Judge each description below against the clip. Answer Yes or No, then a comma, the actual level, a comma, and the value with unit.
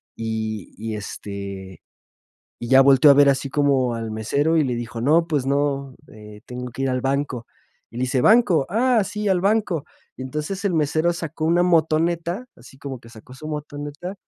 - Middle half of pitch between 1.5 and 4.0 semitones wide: No, average, 5.2 semitones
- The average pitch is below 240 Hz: Yes, medium, 140 Hz